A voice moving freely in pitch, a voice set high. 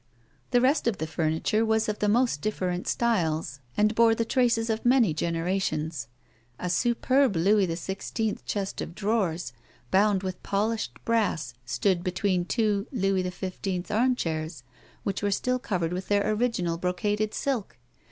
No: average, 4.3 semitones; high, 200 Hz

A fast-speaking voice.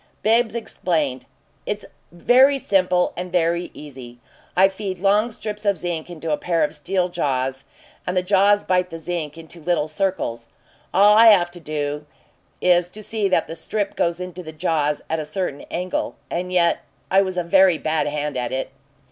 No: average, 180 wpm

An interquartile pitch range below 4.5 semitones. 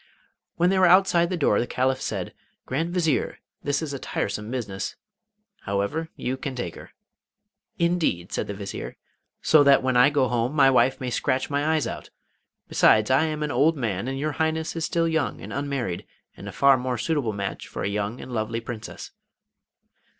No: average, 5.3 semitones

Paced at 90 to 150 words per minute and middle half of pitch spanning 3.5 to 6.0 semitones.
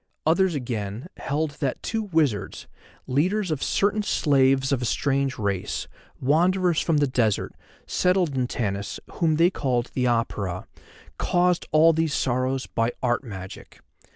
Yes: average, 140 wpm; wide, 5.4 semitones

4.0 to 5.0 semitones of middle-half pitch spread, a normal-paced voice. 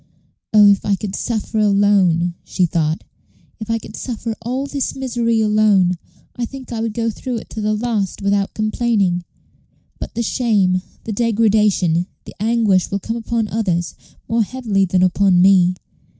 No: average, 3.3 semitones; average, 165 wpm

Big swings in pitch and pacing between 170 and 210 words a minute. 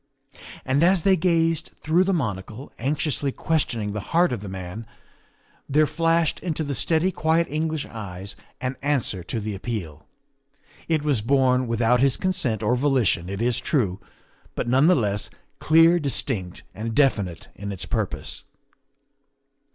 No: wide, 6.9 semitones; average, 150 wpm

